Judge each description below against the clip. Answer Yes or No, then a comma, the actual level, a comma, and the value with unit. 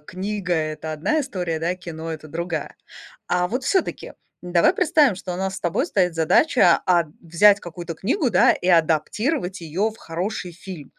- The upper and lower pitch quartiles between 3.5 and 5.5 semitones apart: Yes, average, 3.8 semitones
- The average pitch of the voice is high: No, medium, 180 Hz